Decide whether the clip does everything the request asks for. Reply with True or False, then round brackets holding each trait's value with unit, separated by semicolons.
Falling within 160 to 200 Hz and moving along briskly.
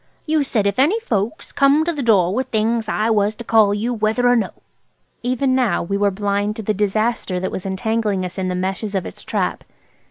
False (215 Hz; 220 wpm)